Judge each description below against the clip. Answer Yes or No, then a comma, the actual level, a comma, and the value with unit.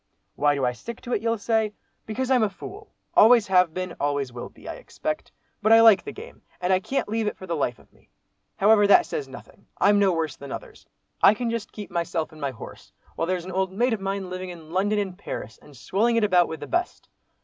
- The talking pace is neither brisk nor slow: No, fast, 245 wpm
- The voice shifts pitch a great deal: No, average, 4.9 semitones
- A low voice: No, high, 195 Hz